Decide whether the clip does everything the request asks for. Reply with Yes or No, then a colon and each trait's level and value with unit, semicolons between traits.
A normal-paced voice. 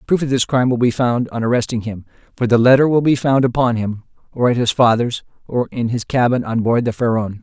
No: fast, 240 wpm